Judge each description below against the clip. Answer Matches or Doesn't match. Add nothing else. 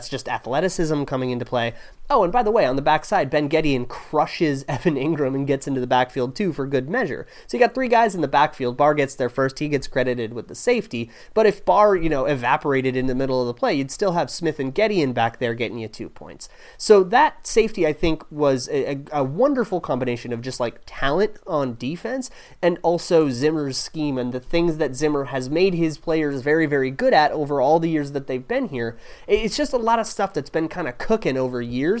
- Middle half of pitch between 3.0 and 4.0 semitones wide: Doesn't match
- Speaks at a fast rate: Matches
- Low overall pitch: Doesn't match